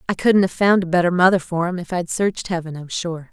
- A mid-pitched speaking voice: Yes, medium, 175 Hz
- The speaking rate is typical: No, fast, 270 wpm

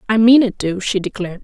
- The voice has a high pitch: Yes, high, 205 Hz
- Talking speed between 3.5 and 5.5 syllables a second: No, 6.4 syllables/s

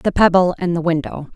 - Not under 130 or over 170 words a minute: No, fast, 220 wpm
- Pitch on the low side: No, medium, 175 Hz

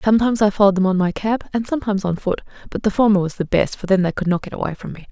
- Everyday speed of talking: No, fast, 305 wpm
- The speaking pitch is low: No, high, 200 Hz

